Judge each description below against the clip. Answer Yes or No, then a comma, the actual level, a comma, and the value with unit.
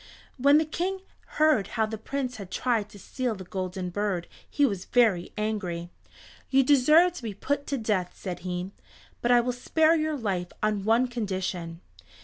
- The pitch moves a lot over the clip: Yes, wide, 6.4 semitones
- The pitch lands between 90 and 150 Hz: No, high, 220 Hz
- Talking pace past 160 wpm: Yes, average, 175 wpm